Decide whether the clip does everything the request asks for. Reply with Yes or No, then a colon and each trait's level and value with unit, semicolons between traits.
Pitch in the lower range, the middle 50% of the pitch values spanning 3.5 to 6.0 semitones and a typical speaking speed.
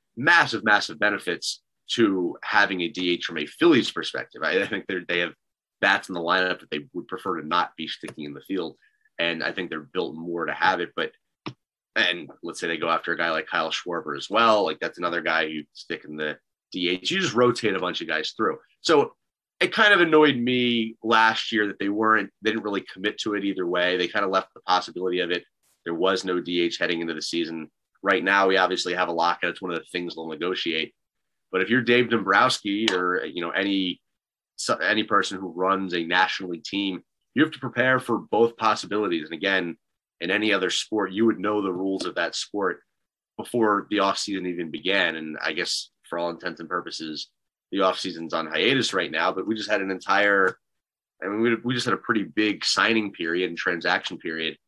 No: very low, 95 Hz; average, 3.8 semitones; fast, 215 wpm